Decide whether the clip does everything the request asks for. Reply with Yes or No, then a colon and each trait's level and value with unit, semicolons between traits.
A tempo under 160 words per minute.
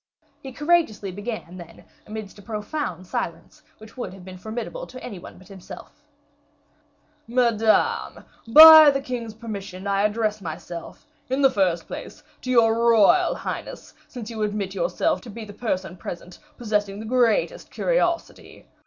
Yes: average, 150 wpm